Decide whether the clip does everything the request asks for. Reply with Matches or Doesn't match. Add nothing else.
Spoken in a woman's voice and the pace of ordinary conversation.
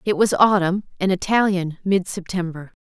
Matches